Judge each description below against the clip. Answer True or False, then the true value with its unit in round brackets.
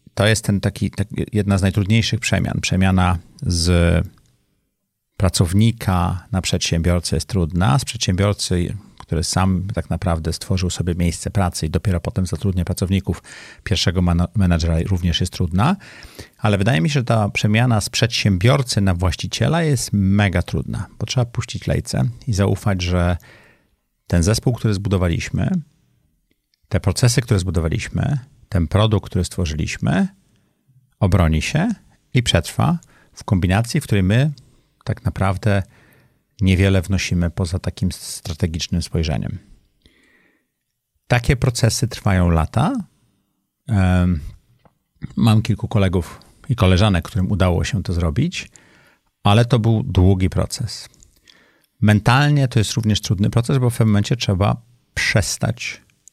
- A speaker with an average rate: True (125 wpm)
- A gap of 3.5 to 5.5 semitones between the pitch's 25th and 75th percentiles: True (4.1 semitones)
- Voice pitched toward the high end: False (100 Hz)